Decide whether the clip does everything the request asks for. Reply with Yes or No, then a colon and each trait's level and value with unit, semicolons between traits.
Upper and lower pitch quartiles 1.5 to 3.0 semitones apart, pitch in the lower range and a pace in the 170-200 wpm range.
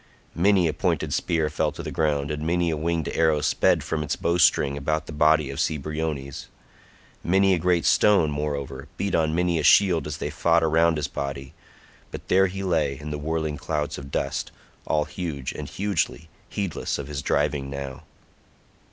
Yes: narrow, 2.6 semitones; very low, 80 Hz; average, 180 wpm